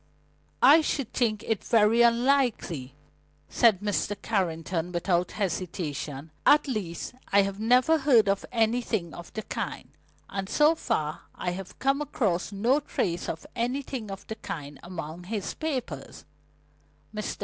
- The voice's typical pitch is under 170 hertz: No, high, 205 Hz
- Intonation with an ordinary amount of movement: No, wide, 5.9 semitones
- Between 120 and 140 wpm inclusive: Yes, slow, 135 wpm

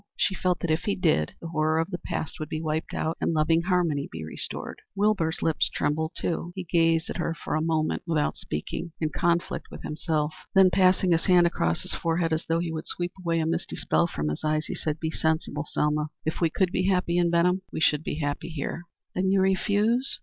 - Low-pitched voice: No, medium, 165 Hz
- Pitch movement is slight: Yes, narrow, 2.3 semitones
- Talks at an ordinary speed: No, fast, 225 wpm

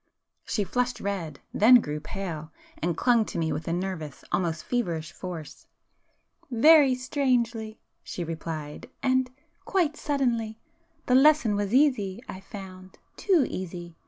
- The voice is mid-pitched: No, high, 205 Hz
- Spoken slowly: Yes, slow, 110 wpm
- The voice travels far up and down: Yes, wide, 6.7 semitones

